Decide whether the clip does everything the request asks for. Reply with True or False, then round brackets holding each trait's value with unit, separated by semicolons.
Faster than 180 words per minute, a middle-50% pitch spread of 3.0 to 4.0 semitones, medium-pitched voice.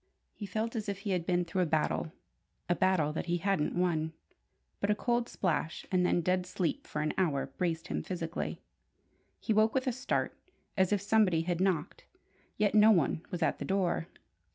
True (195 wpm; 3.6 semitones; 180 Hz)